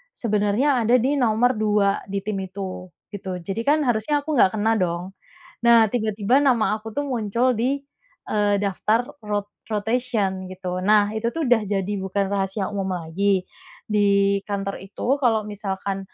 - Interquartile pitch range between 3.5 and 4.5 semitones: No, average, 3.0 semitones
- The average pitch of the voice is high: Yes, high, 210 Hz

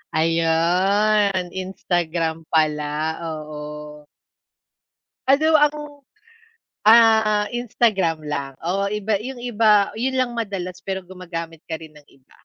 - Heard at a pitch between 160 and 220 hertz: Yes, medium, 185 Hz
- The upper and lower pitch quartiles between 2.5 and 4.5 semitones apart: No, average, 5.1 semitones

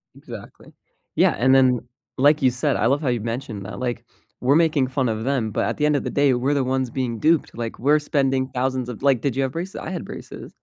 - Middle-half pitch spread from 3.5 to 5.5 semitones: No, narrow, 2.6 semitones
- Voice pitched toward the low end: Yes, low, 130 Hz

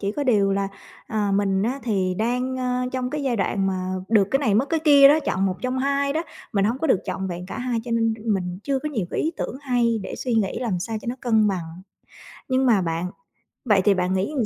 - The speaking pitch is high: Yes, high, 225 Hz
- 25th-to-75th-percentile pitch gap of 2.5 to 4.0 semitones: No, average, 5.0 semitones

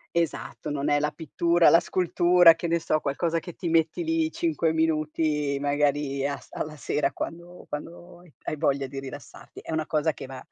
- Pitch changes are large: No, average, 2.8 semitones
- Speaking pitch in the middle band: Yes, medium, 155 Hz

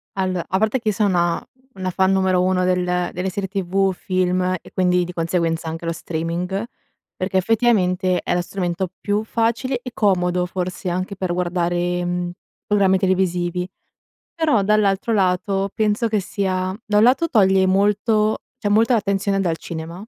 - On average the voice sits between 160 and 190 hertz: Yes, medium, 185 Hz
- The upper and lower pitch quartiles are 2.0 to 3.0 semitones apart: Yes, narrow, 2.3 semitones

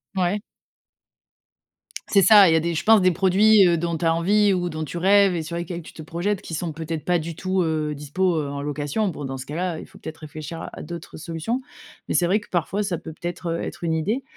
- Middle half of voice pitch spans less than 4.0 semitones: Yes, average, 3.1 semitones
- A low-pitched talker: No, medium, 170 Hz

